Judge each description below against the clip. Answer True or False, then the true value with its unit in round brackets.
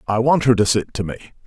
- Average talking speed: False (285 wpm)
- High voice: False (115 Hz)